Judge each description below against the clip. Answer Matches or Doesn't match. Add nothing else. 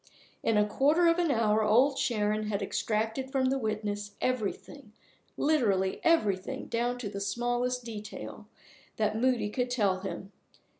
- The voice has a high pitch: Matches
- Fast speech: Doesn't match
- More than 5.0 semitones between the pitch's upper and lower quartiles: Doesn't match